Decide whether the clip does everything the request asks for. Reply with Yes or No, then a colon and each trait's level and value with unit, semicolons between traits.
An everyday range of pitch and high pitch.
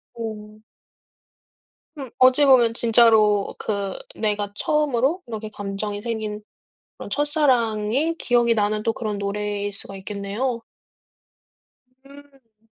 Yes: average, 3.5 semitones; high, 220 Hz